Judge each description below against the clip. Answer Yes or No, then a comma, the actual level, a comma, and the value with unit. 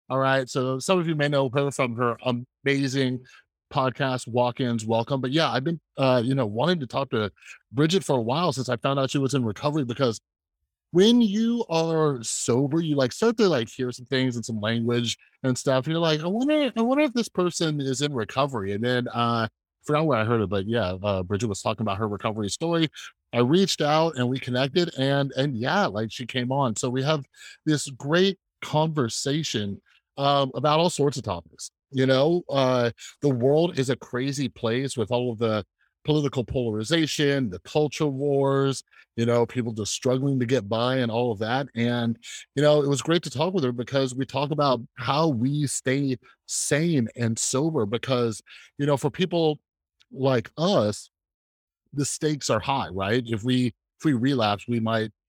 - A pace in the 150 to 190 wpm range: No, average, 200 wpm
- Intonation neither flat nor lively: Yes, average, 3.9 semitones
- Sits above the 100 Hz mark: Yes, low, 130 Hz